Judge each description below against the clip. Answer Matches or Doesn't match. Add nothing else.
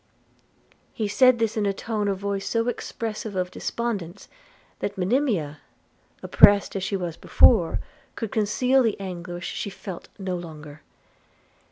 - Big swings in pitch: Doesn't match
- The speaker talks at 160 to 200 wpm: Doesn't match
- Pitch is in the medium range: Doesn't match